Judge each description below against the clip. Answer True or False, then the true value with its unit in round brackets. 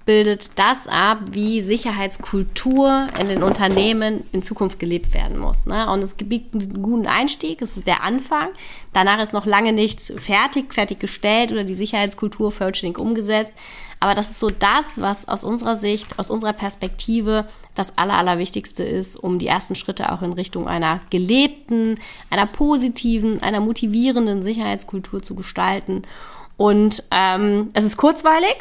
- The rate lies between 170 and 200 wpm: False (150 wpm)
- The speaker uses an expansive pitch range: False (2.7 semitones)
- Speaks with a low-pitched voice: False (210 Hz)